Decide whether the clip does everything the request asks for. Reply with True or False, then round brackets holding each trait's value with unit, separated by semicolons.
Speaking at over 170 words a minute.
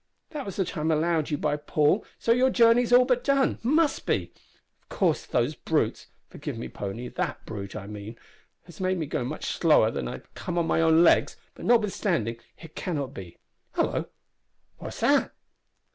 True (190 wpm)